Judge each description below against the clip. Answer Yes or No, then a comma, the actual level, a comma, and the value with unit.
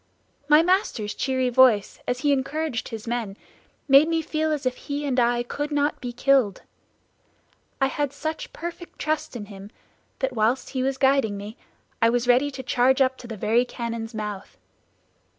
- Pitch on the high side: Yes, very high, 255 Hz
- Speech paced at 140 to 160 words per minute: No, average, 175 wpm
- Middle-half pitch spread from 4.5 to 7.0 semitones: No, average, 3.7 semitones